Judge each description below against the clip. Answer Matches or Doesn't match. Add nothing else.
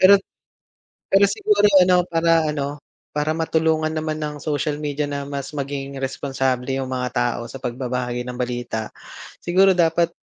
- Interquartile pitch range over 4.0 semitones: Doesn't match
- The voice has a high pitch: Doesn't match